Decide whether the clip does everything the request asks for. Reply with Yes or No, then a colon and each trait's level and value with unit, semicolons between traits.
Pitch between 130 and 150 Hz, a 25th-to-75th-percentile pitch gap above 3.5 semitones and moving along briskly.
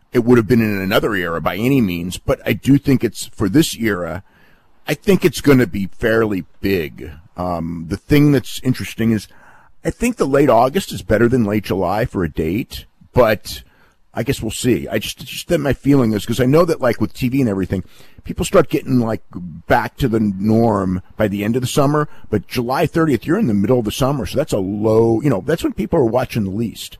No: low, 115 Hz; average, 4.9 semitones; fast, 230 wpm